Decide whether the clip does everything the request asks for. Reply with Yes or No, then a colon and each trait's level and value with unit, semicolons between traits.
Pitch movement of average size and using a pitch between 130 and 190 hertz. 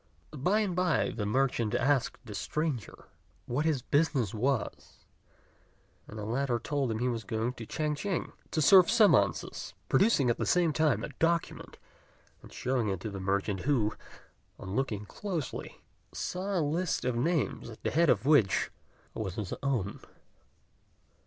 No: wide, 6.4 semitones; low, 135 Hz